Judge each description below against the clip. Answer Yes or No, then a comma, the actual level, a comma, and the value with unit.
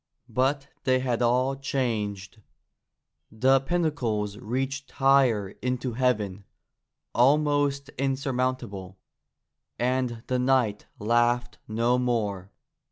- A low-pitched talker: Yes, low, 125 Hz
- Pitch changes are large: No, average, 3.2 semitones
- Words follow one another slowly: Yes, slow, 90 wpm